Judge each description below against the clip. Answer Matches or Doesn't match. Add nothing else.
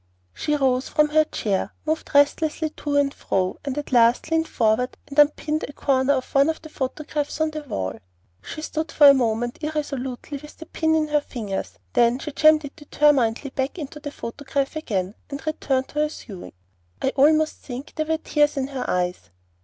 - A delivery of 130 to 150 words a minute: Doesn't match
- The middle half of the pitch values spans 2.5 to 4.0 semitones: Matches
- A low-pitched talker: Doesn't match